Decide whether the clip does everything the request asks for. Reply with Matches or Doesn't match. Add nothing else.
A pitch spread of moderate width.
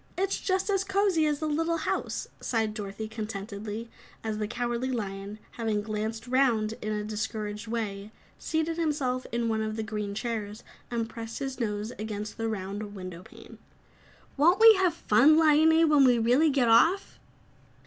Doesn't match